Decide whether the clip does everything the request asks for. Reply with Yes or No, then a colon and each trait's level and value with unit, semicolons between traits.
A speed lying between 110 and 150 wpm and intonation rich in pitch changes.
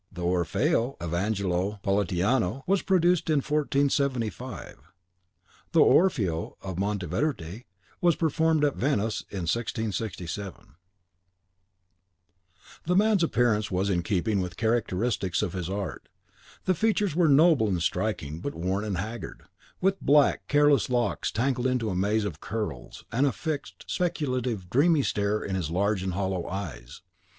Yes: average, 140 wpm; wide, 7.3 semitones